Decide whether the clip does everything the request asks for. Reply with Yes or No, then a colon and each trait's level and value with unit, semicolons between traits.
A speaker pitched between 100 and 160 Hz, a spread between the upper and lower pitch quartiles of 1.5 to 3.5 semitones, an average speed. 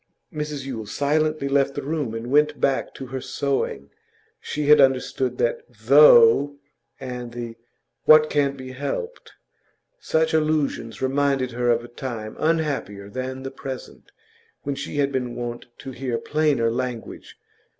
Yes: low, 135 Hz; average, 3.1 semitones; average, 150 wpm